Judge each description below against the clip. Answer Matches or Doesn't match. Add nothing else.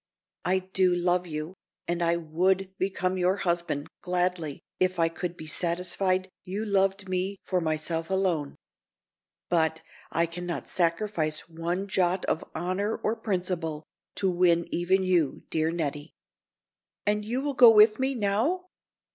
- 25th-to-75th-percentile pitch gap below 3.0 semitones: Matches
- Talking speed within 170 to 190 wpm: Doesn't match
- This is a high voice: Doesn't match